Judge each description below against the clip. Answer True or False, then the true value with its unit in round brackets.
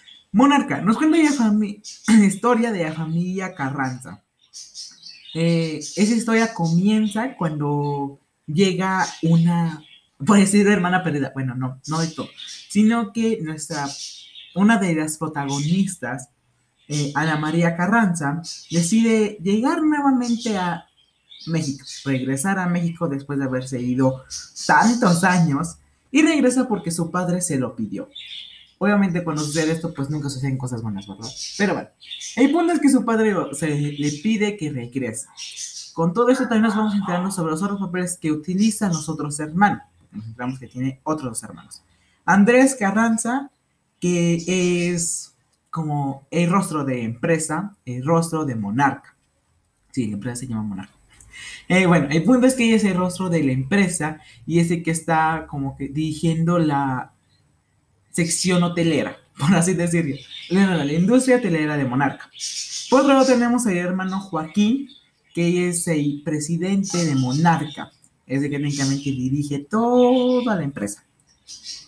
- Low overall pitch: False (170 Hz)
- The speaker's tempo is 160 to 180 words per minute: False (150 wpm)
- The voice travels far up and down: True (6.2 semitones)